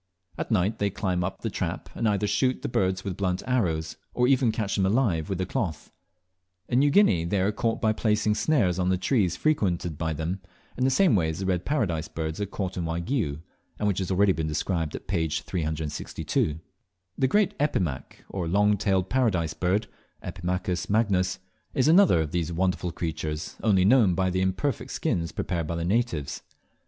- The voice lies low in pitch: Yes, very low, 95 Hz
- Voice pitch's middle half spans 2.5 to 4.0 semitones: No, average, 4.4 semitones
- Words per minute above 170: Yes, average, 190 wpm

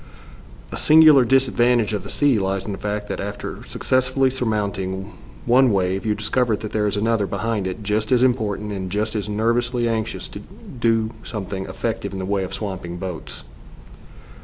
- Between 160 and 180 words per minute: Yes, average, 175 wpm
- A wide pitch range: No, average, 3.3 semitones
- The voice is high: No, low, 105 Hz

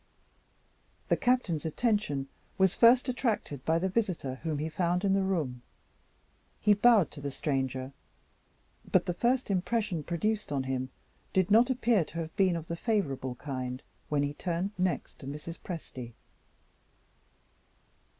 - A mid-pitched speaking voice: Yes, medium, 170 Hz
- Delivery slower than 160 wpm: Yes, average, 145 wpm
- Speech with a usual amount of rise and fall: No, wide, 6.5 semitones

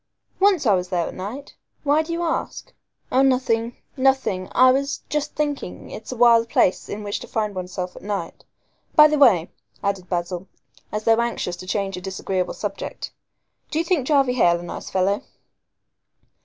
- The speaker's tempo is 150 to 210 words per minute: Yes, average, 180 wpm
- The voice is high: Yes, high, 225 Hz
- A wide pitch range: Yes, wide, 6.6 semitones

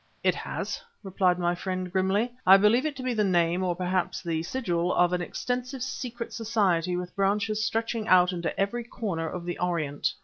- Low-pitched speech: No, high, 190 Hz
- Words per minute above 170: Yes, average, 190 wpm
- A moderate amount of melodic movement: Yes, average, 4.1 semitones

